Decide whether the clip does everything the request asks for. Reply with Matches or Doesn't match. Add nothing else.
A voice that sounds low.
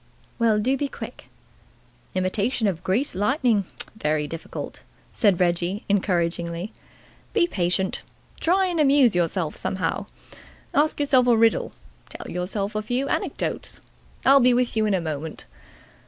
Doesn't match